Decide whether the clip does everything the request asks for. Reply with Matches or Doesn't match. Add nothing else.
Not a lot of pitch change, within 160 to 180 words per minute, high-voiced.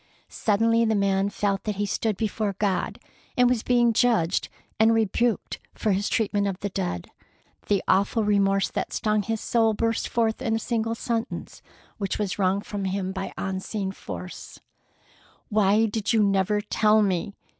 Matches